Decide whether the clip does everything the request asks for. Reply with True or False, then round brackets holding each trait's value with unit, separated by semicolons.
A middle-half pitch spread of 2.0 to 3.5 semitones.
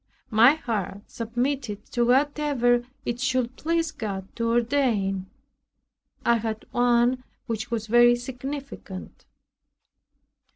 True (2.8 semitones)